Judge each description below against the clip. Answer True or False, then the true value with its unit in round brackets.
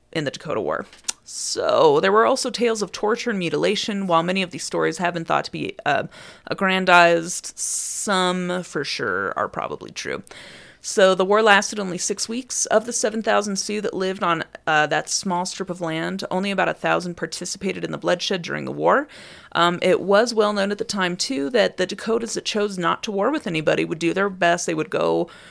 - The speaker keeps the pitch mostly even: False (3.4 semitones)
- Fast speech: True (210 wpm)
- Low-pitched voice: False (190 Hz)